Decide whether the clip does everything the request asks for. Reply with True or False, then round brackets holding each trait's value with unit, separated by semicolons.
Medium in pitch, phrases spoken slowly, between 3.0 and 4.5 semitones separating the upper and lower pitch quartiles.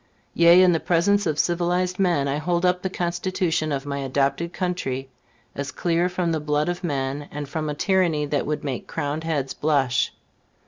False (160 Hz; 185 wpm; 3.7 semitones)